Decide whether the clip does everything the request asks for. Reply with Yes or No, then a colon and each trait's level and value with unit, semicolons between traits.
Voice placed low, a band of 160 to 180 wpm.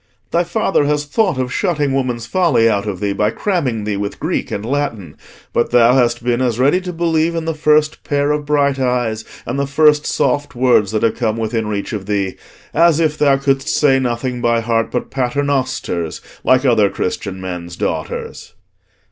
No: low, 130 Hz; average, 190 wpm